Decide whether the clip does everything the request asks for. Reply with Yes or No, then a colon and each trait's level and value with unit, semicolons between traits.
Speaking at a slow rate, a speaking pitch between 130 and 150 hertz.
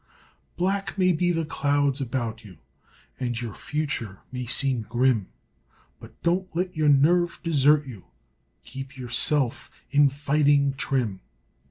Yes: slow, 130 wpm; medium, 140 Hz